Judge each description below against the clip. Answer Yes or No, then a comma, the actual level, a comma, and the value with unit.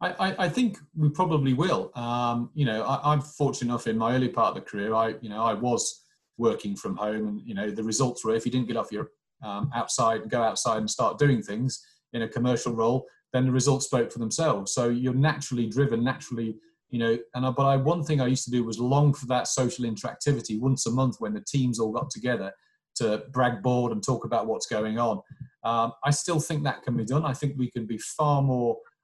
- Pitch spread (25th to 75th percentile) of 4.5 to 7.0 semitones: No, average, 3.6 semitones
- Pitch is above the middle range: No, low, 125 Hz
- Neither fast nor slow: No, fast, 240 wpm